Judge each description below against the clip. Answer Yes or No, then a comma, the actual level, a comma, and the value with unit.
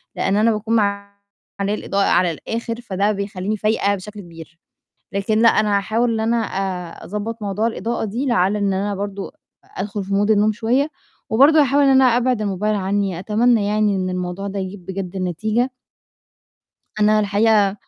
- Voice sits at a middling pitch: No, high, 205 Hz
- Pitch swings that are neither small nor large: No, narrow, 2.3 semitones